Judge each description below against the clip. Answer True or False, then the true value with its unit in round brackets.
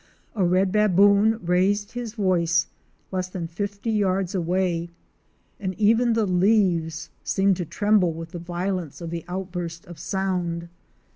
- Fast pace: False (140 wpm)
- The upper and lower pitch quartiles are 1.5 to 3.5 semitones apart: True (2.9 semitones)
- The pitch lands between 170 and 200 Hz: True (185 Hz)